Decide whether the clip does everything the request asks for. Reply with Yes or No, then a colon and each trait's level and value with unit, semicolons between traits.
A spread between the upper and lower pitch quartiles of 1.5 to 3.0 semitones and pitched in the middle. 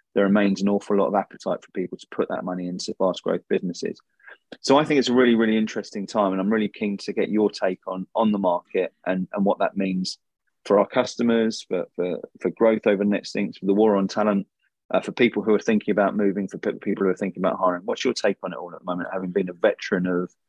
No: narrow, 2.5 semitones; low, 100 Hz